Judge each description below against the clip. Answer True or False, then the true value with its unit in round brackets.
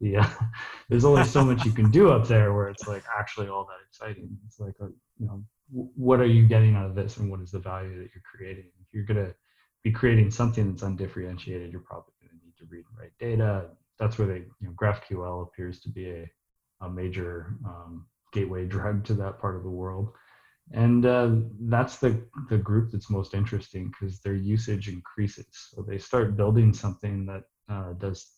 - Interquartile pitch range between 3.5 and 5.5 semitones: False (3.1 semitones)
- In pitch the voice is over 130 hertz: False (105 Hz)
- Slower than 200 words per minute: False (205 wpm)